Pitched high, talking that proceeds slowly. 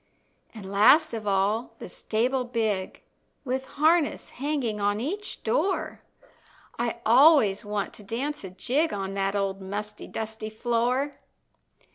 Yes: high, 225 Hz; slow, 130 wpm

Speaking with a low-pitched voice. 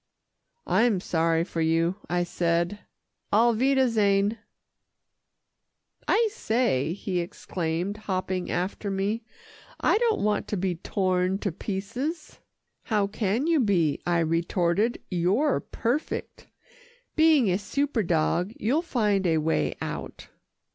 No: high, 200 Hz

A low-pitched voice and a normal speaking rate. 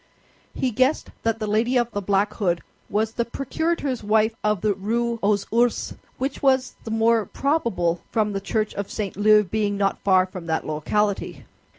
No: high, 215 Hz; average, 180 wpm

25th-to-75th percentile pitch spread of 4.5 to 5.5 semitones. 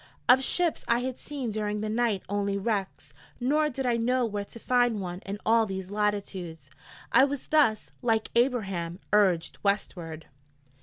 No: average, 3.9 semitones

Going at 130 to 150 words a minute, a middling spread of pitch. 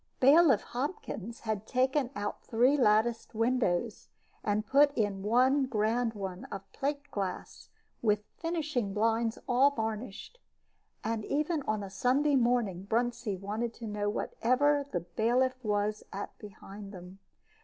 Yes: slow, 135 wpm; average, 3.9 semitones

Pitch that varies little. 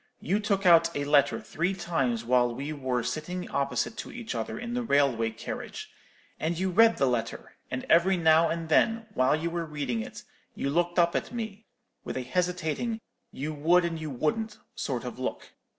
No: average, 5.1 semitones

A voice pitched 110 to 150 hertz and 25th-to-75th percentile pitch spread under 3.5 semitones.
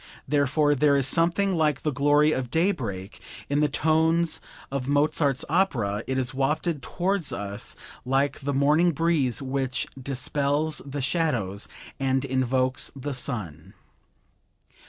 Yes: medium, 140 Hz; average, 3.1 semitones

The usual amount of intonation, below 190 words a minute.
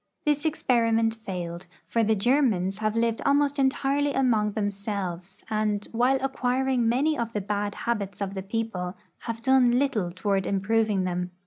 Yes: average, 4.2 semitones; average, 155 wpm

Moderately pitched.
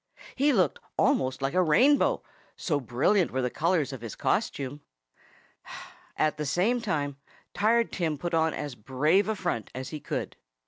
Yes: medium, 155 Hz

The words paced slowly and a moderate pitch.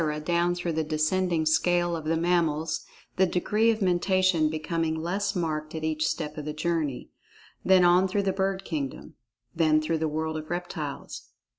No: average, 170 wpm; medium, 165 Hz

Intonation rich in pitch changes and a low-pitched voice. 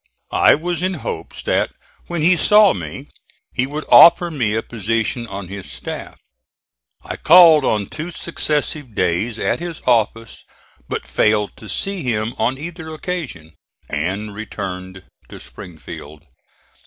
Yes: wide, 8.2 semitones; low, 115 Hz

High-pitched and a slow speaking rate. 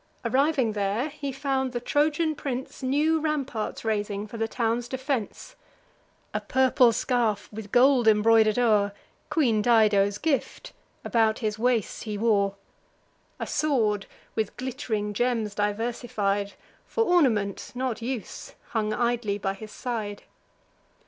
Yes: high, 230 Hz; slow, 125 wpm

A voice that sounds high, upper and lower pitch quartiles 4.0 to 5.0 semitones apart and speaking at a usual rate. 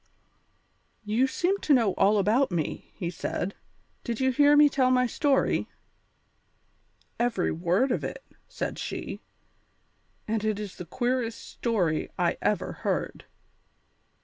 No: high, 230 Hz; average, 4.7 semitones; slow, 130 wpm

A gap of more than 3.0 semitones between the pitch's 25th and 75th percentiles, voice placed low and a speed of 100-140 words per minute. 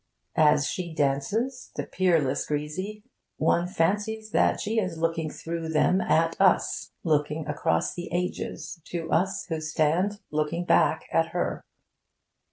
No: average, 3.4 semitones; medium, 165 Hz; slow, 135 wpm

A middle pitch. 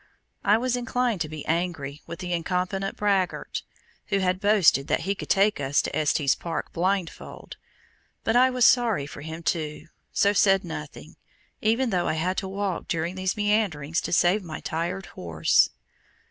Yes: medium, 180 Hz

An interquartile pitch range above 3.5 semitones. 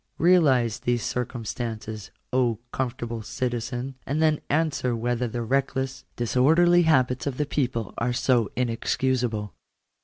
No: narrow, 2.5 semitones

